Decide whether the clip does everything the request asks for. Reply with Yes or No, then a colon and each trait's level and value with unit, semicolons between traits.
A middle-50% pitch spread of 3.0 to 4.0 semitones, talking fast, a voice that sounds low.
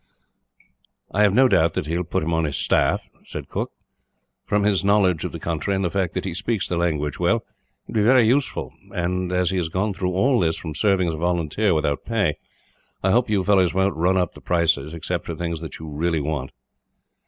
Yes: average, 3.3 semitones; fast, 225 wpm; very low, 90 Hz